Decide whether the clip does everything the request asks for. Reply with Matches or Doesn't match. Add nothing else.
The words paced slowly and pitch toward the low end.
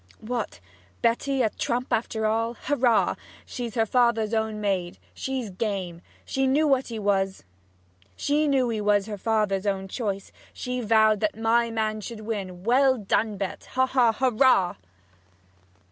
Doesn't match